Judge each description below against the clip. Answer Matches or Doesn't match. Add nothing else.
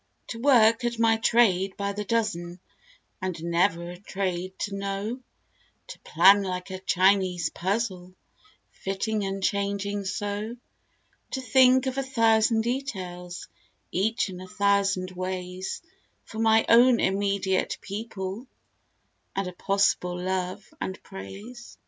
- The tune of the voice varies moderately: Matches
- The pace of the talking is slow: Matches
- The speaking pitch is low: Doesn't match